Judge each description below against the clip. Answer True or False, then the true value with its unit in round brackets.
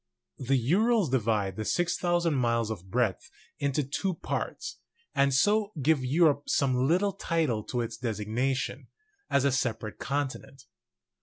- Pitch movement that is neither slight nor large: True (4.9 semitones)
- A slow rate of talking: True (130 wpm)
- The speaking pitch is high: False (135 Hz)